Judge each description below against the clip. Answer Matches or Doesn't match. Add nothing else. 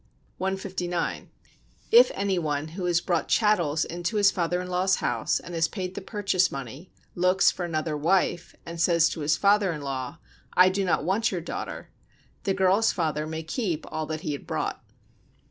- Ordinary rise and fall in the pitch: Matches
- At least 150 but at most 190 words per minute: Matches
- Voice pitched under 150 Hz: Doesn't match